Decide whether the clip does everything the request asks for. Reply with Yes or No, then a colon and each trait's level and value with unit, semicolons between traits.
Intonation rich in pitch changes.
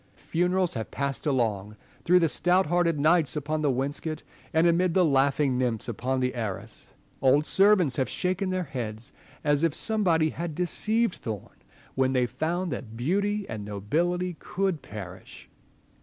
Yes: wide, 5.8 semitones